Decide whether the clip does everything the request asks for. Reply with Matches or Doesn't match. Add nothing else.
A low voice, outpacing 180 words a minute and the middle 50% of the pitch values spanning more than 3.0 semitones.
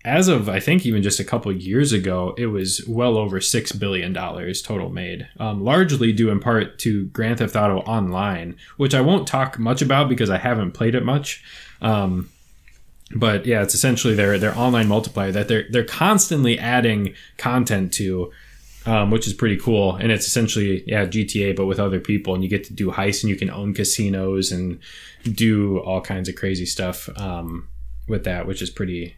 Matches